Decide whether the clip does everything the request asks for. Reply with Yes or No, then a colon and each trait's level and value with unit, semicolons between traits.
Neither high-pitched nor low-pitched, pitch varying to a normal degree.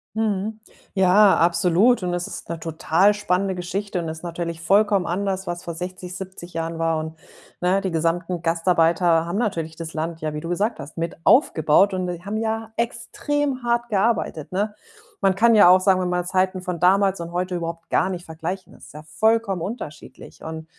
Yes: medium, 180 Hz; average, 3.2 semitones